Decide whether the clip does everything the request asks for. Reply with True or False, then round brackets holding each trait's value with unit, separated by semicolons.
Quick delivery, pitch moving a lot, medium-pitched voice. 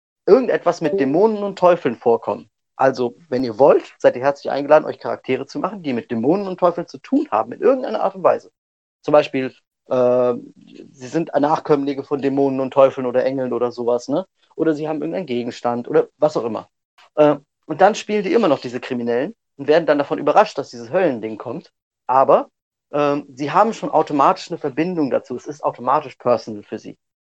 False (195 wpm; 4.0 semitones; 145 Hz)